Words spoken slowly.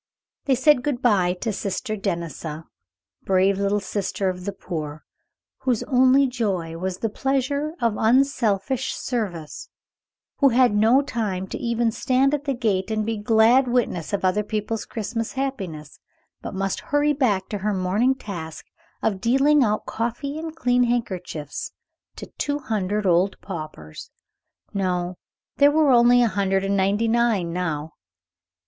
No: average, 150 wpm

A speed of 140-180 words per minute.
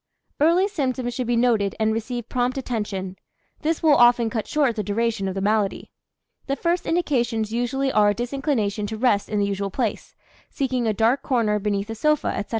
No: average, 190 wpm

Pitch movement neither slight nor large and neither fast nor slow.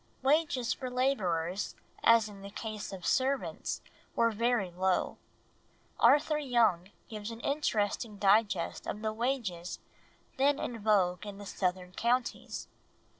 No: average, 4.4 semitones; slow, 125 wpm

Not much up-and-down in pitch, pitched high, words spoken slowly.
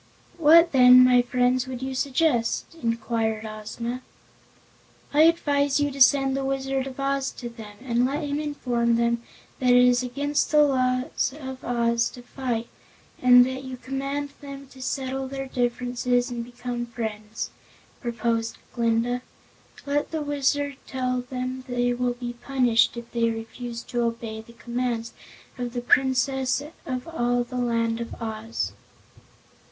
No: narrow, 2.3 semitones; very high, 250 Hz; average, 150 wpm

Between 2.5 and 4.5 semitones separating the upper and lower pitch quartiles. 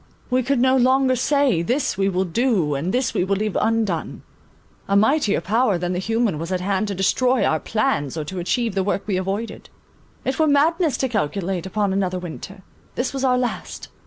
No: wide, 5.5 semitones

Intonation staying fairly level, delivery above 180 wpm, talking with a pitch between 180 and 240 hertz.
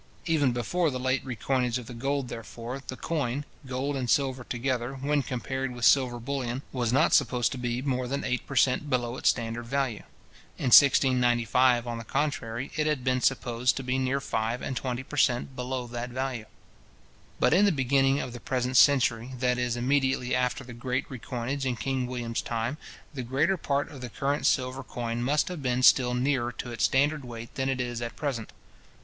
No: narrow, 2.1 semitones; average, 195 wpm; low, 130 Hz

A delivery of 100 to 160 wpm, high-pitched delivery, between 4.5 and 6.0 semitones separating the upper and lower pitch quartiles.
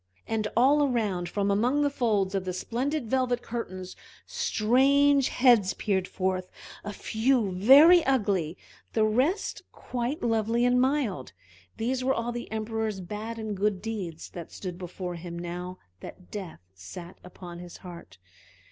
Yes: average, 150 wpm; high, 215 Hz; average, 5.2 semitones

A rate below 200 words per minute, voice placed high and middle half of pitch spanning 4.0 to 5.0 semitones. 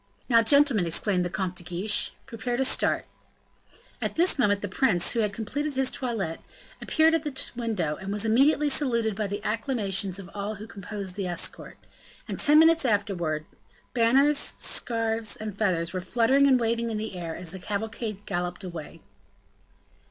Yes: average, 170 wpm; high, 215 Hz; average, 4.5 semitones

